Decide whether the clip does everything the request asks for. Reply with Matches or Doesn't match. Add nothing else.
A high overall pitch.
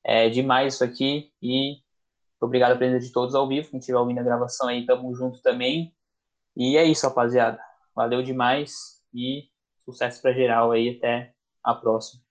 Doesn't match